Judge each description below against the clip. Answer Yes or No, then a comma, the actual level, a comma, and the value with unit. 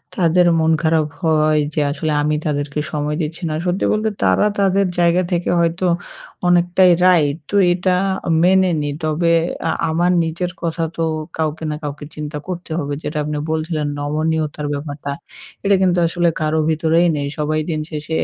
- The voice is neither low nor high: Yes, medium, 160 Hz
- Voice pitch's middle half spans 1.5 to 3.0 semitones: Yes, narrow, 2.6 semitones